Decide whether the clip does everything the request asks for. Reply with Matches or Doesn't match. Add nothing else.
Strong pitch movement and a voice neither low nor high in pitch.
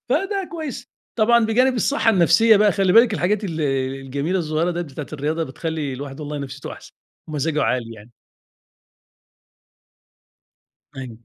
Matches